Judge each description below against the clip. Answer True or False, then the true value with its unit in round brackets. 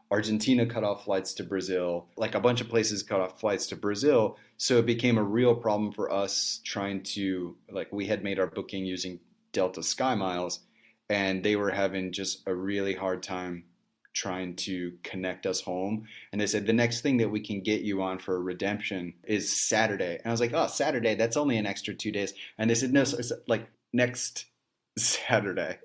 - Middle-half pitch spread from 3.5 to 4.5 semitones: False (3.1 semitones)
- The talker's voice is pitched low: True (100 Hz)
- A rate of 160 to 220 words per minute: True (205 wpm)